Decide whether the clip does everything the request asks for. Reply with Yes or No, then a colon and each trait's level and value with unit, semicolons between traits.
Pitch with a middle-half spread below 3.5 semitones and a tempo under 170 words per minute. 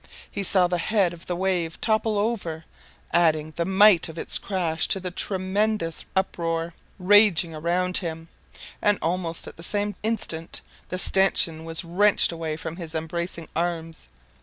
Yes: average, 2.8 semitones; average, 155 wpm